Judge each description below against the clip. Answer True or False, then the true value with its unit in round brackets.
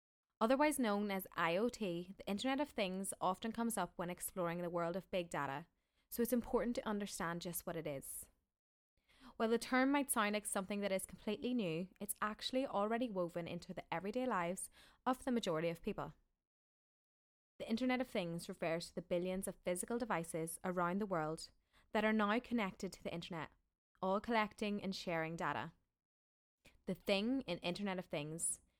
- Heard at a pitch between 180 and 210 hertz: True (190 Hz)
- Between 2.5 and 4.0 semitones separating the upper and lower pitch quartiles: False (4.8 semitones)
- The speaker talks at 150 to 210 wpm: True (175 wpm)